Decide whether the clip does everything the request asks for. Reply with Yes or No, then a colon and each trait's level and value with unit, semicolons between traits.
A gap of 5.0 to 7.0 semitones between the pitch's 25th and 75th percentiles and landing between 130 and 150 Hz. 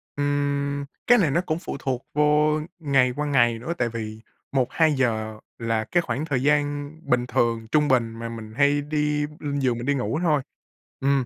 No: average, 3.8 semitones; medium, 140 Hz